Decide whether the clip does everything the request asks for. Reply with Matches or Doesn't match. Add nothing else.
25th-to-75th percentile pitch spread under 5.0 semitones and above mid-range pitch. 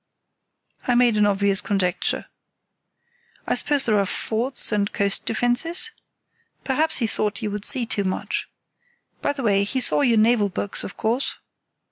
Matches